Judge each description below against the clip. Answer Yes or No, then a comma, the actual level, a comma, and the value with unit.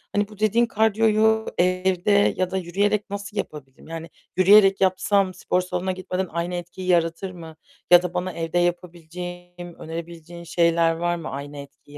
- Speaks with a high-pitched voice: No, medium, 180 Hz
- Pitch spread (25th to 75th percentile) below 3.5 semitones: Yes, narrow, 2.4 semitones